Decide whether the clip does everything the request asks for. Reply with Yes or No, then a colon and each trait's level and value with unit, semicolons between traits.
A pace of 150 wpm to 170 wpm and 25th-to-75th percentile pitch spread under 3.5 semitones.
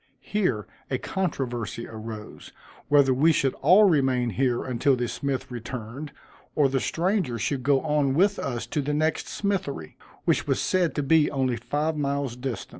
No: average, 165 wpm; average, 4.0 semitones